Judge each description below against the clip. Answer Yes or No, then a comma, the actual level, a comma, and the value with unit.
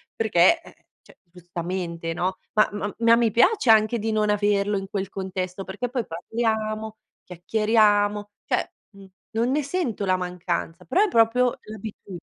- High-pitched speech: Yes, high, 210 Hz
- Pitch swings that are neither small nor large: Yes, average, 3.2 semitones